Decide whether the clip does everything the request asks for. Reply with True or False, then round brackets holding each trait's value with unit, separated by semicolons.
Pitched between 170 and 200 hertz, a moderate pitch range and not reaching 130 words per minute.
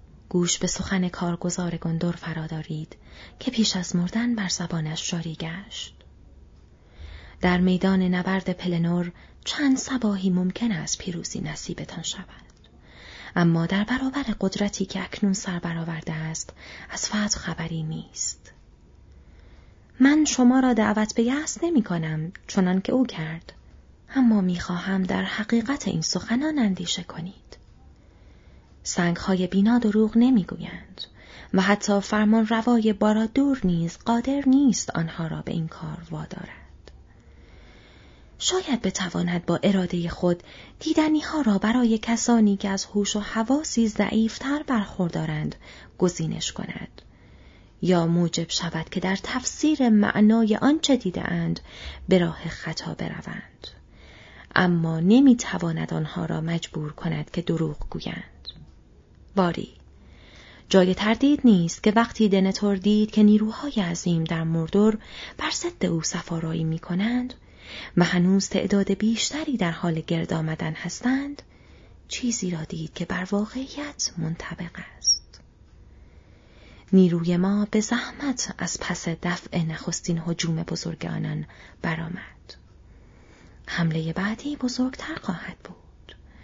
True (185 Hz; 5.0 semitones; 120 wpm)